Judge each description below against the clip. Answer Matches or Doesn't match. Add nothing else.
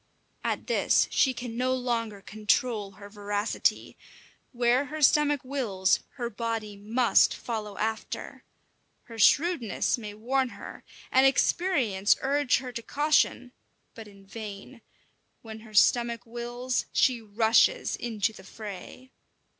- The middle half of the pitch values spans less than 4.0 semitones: Matches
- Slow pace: Matches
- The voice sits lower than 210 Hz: Doesn't match